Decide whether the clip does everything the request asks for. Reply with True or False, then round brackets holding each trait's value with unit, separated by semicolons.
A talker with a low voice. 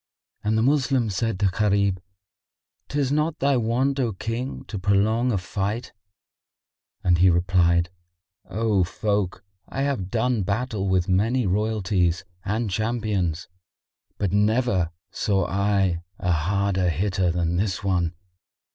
True (100 Hz)